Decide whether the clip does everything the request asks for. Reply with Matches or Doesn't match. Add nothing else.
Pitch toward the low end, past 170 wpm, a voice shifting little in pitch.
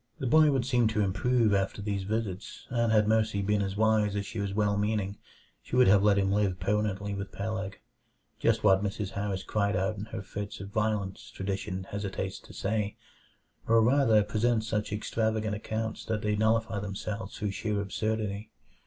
Matches